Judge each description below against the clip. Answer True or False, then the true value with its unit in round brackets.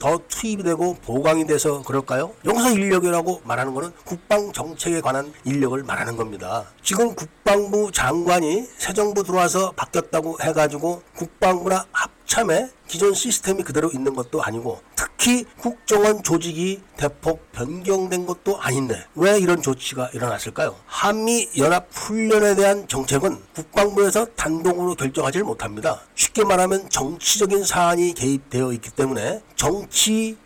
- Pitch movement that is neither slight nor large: False (5.7 semitones)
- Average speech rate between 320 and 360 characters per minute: True (340 characters per minute)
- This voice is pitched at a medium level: True (175 Hz)